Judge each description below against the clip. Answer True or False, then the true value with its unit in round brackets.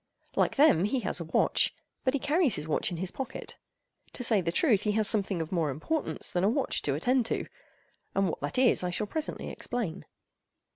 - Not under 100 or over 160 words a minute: False (205 wpm)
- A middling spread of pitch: False (6.7 semitones)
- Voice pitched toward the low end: False (210 Hz)